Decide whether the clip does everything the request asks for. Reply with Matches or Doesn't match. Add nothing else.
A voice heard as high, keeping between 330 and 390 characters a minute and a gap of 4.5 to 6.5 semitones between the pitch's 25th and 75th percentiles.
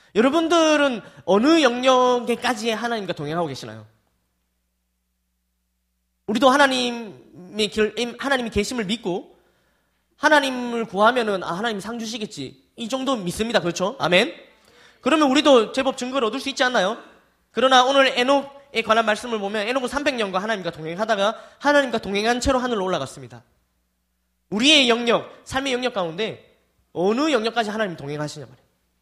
Doesn't match